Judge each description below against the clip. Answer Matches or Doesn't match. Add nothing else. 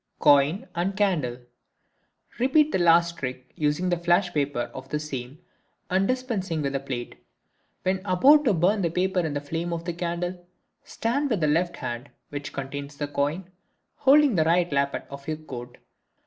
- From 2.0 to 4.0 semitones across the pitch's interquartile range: Doesn't match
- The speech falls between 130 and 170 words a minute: Matches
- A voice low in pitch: Doesn't match